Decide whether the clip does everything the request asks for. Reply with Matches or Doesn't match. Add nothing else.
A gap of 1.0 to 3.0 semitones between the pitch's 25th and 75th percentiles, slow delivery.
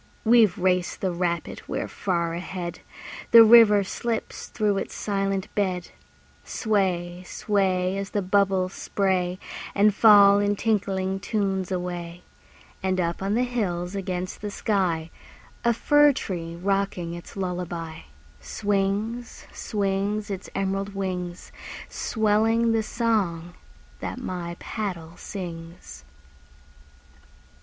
Matches